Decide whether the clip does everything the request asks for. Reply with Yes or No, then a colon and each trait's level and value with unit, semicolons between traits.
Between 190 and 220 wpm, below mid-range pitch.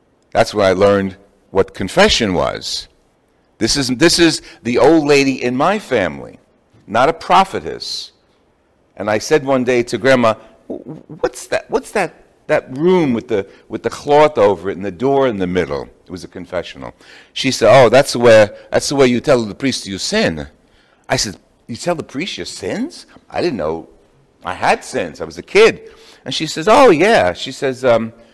Yes: average, 195 wpm; low, 130 Hz